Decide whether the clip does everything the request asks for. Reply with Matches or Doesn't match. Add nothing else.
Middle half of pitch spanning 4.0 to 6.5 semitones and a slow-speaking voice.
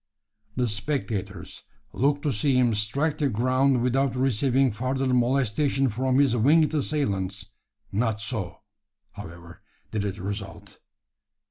Matches